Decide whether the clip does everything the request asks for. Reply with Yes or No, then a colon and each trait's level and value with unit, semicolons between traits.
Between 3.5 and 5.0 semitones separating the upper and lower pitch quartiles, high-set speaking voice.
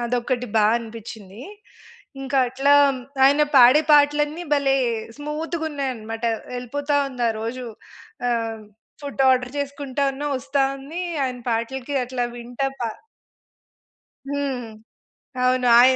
No: average, 2.8 semitones; very high, 260 Hz